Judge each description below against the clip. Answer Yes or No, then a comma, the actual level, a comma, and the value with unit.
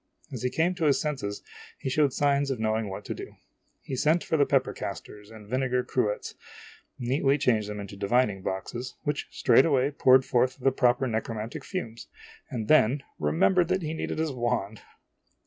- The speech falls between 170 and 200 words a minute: Yes, average, 180 wpm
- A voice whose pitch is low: Yes, low, 125 Hz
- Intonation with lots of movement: No, average, 4.5 semitones